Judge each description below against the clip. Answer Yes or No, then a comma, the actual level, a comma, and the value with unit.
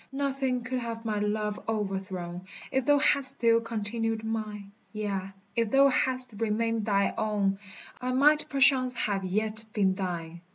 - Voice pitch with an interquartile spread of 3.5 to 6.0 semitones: Yes, average, 4.0 semitones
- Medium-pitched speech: No, high, 220 Hz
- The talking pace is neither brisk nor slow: Yes, average, 150 wpm